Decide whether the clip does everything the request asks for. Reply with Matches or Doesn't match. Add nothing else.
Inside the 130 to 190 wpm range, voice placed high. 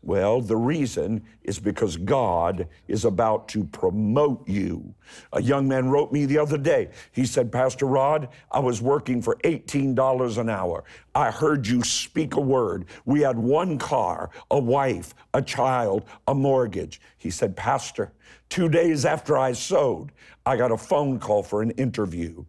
Doesn't match